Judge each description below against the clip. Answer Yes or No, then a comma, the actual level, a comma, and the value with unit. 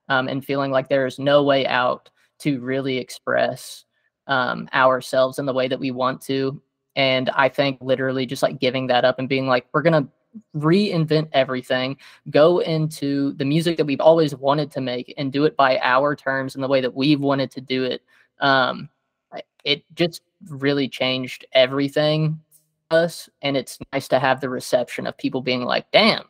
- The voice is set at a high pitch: No, low, 135 Hz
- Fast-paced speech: No, average, 190 wpm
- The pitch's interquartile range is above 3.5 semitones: No, narrow, 2.6 semitones